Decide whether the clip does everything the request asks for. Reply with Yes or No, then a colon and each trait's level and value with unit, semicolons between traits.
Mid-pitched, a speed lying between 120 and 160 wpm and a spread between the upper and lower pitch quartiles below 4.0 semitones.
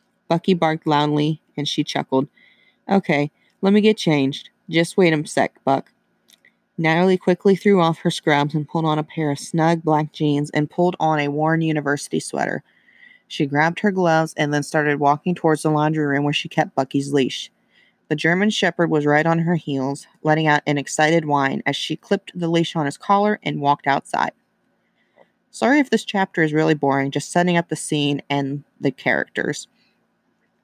No: medium, 155 Hz; average, 185 wpm; average, 3.1 semitones